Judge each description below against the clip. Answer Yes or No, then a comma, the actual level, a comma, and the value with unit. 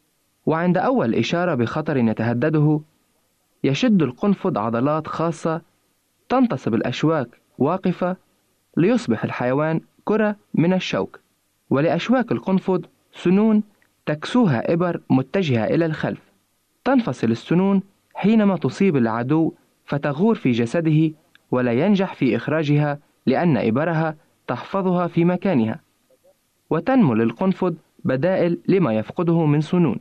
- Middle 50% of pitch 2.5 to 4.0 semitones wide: No, average, 4.7 semitones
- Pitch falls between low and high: Yes, medium, 170 Hz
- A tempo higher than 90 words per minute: Yes, average, 100 wpm